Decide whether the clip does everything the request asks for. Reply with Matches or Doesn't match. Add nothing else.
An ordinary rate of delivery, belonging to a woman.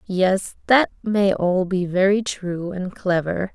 Matches